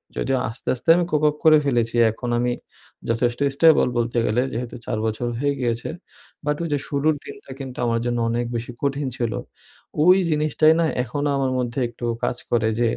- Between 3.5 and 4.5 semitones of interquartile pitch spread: Yes, average, 3.8 semitones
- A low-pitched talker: Yes, low, 125 Hz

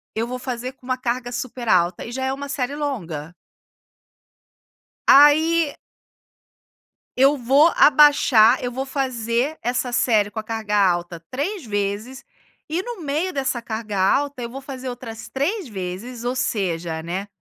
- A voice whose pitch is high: Yes, high, 245 Hz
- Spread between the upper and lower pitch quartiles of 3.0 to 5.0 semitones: Yes, average, 4.3 semitones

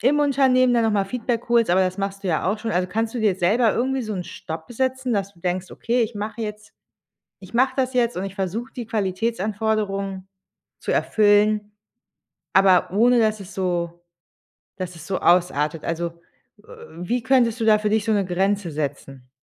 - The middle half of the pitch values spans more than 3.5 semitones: Yes, average, 4.0 semitones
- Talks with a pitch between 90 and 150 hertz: No, high, 210 Hz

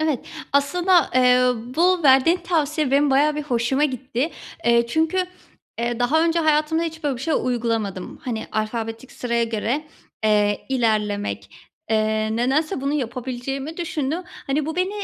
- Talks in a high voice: Yes, very high, 270 Hz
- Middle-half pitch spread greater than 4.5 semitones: Yes, average, 4.9 semitones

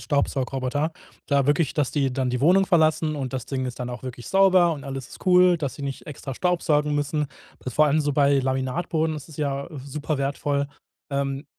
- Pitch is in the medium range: Yes, medium, 145 Hz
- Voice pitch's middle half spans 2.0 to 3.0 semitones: Yes, narrow, 2.6 semitones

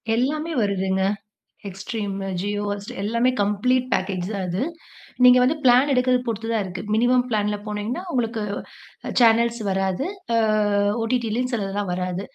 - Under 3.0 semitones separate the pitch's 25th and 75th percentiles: No, average, 4.0 semitones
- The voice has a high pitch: Yes, high, 220 Hz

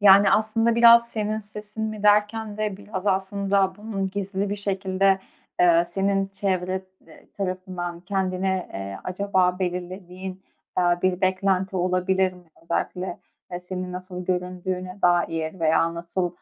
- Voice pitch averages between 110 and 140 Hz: No, high, 190 Hz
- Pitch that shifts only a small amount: Yes, narrow, 1.8 semitones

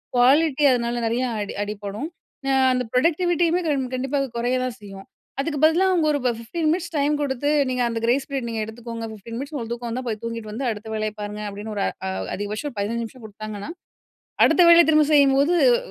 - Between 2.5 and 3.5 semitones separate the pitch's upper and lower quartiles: No, average, 4.7 semitones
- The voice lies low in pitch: No, high, 245 Hz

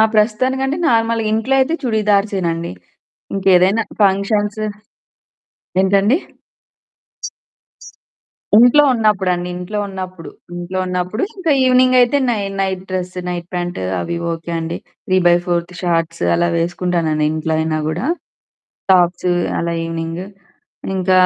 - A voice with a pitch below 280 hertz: Yes, medium, 185 Hz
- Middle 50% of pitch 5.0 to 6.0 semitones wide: No, average, 3.8 semitones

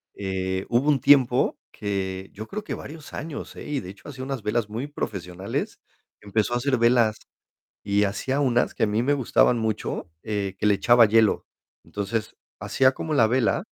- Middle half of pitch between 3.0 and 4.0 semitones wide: No, average, 4.5 semitones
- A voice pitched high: No, low, 115 Hz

